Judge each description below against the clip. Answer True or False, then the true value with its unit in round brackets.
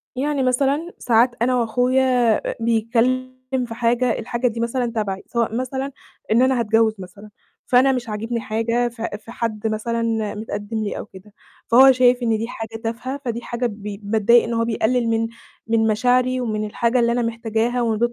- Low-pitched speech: False (235 Hz)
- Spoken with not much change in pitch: True (2.1 semitones)